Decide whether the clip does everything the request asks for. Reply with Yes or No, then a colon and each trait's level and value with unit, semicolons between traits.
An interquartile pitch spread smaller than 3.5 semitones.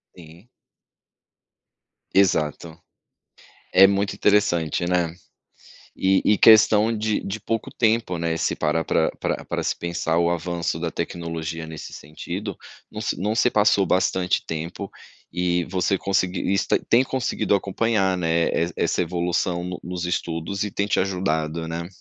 Yes: average, 3.0 semitones